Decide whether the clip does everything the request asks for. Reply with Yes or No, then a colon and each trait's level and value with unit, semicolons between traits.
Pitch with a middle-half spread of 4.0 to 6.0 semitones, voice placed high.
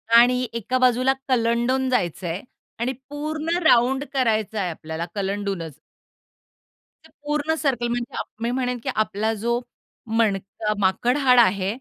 Yes: average, 4.3 semitones; high, 235 Hz